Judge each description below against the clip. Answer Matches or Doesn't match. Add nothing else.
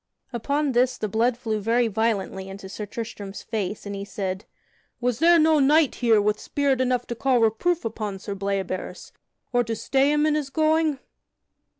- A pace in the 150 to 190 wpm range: Matches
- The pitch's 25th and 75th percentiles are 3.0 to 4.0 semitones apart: Doesn't match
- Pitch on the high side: Matches